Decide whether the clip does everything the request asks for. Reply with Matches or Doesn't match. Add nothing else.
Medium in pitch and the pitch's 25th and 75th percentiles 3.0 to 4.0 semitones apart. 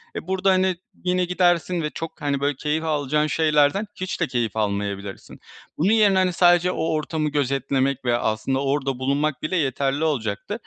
Doesn't match